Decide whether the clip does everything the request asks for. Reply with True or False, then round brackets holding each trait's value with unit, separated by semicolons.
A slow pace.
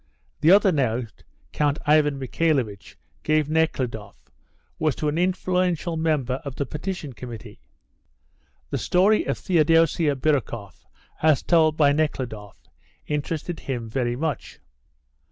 True (120 wpm)